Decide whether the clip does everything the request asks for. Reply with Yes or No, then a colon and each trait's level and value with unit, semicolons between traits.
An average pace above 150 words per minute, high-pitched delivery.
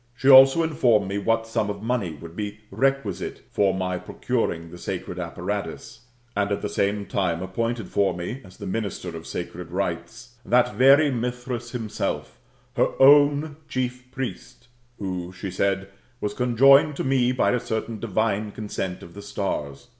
No: average, 165 wpm; low, 110 Hz